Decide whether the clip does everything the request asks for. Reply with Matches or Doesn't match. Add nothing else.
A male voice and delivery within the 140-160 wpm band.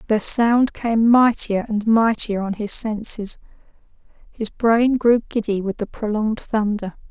Doesn't match